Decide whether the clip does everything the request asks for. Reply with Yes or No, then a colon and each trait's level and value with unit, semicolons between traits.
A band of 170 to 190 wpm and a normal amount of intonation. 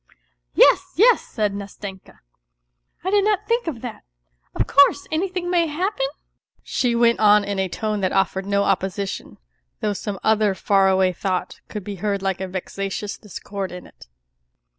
No: average, 180 wpm; wide, 5.8 semitones